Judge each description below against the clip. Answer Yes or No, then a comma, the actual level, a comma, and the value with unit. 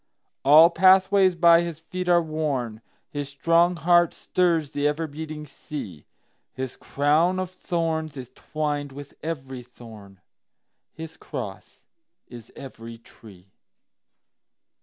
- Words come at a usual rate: No, slow, 105 wpm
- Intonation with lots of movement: No, average, 4.3 semitones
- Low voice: No, medium, 150 Hz